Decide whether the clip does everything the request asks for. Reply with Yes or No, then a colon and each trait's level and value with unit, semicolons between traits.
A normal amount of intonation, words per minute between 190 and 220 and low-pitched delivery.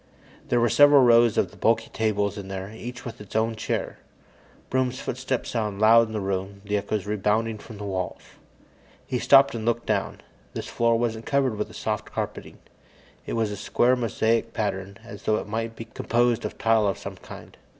No: narrow, 2.2 semitones; average, 195 wpm; low, 110 Hz